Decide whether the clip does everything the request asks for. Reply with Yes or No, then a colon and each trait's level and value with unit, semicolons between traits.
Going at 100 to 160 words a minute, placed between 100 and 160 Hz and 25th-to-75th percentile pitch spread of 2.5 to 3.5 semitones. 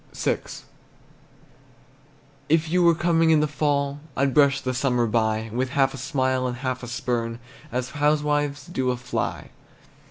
Yes: average, 155 wpm; low, 135 Hz; average, 2.9 semitones